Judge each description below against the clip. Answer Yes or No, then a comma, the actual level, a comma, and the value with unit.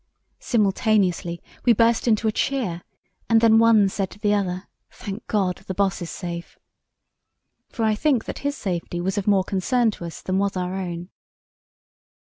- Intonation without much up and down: No, average, 3.4 semitones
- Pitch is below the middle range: No, high, 200 Hz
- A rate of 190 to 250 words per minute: No, average, 170 wpm